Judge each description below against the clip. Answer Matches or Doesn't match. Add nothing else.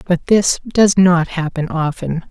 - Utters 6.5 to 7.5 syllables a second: Doesn't match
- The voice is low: Doesn't match